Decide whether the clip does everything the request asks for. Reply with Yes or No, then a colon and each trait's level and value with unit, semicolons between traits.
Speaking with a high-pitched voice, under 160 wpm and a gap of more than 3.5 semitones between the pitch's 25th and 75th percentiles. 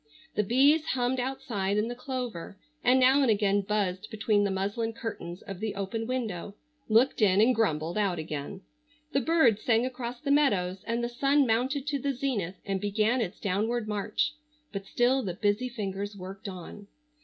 No: high, 220 Hz; average, 180 wpm; average, 4.2 semitones